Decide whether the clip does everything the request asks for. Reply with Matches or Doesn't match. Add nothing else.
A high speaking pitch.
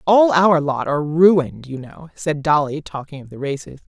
Doesn't match